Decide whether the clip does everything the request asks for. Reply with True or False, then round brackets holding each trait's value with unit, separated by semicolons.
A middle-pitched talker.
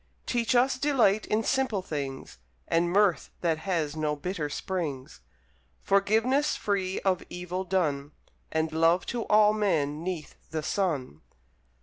True (180 Hz)